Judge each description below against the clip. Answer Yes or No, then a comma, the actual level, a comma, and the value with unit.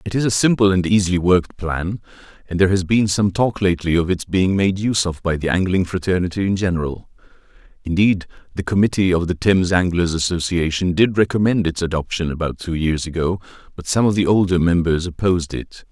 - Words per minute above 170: Yes, average, 190 wpm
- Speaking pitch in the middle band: No, very low, 90 Hz